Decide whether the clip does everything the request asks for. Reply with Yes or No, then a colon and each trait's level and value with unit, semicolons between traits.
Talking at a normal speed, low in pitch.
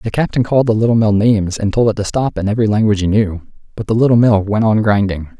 No: fast, 265 wpm; low, 110 Hz